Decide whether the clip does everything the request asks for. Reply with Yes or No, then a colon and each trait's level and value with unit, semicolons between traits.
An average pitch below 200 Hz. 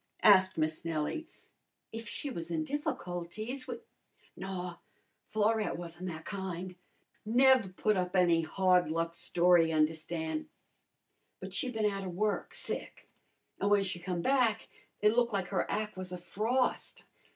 Yes: medium, 185 Hz